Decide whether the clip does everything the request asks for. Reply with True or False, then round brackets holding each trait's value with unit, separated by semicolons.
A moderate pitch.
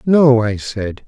False (120 Hz)